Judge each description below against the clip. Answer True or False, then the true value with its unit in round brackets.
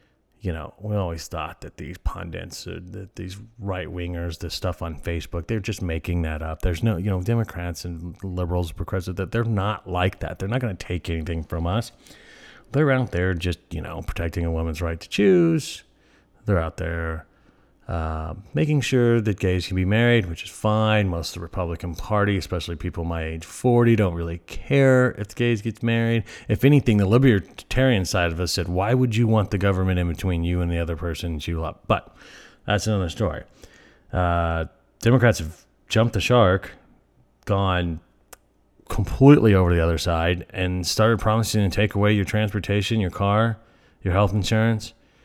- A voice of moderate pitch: False (95 Hz)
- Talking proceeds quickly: False (180 wpm)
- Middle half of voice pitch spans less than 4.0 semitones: False (4.3 semitones)